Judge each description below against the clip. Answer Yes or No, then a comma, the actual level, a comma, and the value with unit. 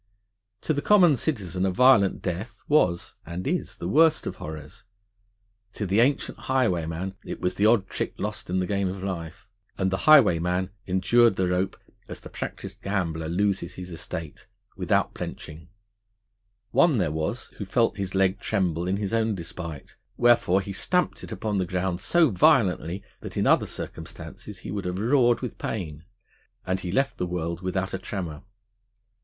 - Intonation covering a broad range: No, average, 4.0 semitones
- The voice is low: Yes, very low, 95 Hz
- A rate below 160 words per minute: No, average, 170 wpm